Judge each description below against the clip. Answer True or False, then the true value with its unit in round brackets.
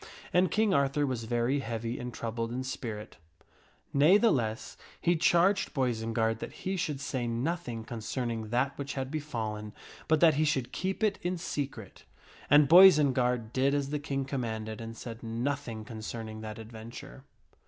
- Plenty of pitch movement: False (4.6 semitones)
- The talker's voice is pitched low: True (125 Hz)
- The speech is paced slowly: False (155 wpm)